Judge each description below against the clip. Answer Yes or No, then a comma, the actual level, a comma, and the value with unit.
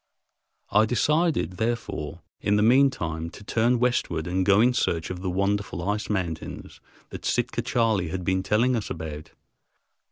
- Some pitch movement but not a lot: Yes, average, 4.9 semitones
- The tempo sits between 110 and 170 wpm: Yes, average, 160 wpm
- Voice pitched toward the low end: Yes, low, 100 Hz